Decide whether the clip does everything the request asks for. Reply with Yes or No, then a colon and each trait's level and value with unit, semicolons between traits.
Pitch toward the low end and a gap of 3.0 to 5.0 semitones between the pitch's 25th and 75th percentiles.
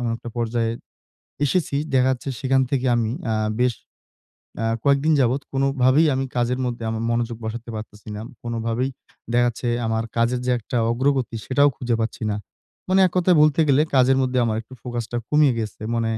No: low, 125 Hz; narrow, 2.6 semitones